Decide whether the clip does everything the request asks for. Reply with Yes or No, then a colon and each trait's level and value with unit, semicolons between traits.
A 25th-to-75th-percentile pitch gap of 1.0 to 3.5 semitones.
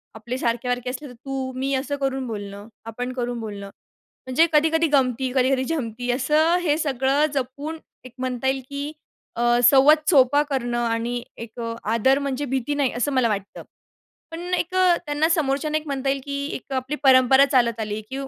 Yes: average, 2.9 semitones